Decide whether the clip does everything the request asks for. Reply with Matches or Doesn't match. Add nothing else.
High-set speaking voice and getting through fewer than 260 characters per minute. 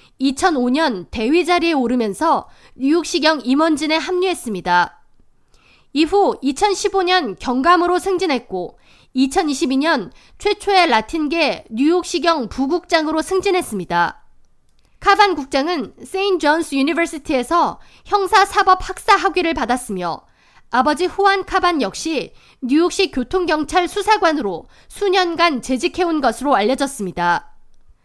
Doesn't match